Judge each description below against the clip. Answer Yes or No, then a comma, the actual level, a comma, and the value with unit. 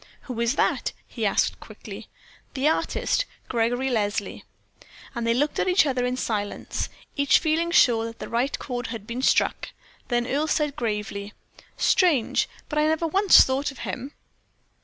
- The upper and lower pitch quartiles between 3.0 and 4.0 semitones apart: No, average, 4.5 semitones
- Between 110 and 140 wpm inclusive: No, average, 160 wpm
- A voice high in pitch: Yes, very high, 255 Hz